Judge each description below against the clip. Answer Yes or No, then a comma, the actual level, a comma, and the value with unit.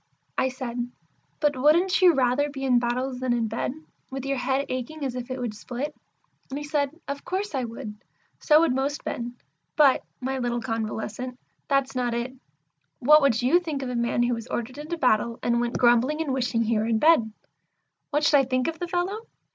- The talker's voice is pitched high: Yes, very high, 255 Hz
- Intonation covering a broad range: No, average, 3.4 semitones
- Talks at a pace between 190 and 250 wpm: Yes, fast, 205 wpm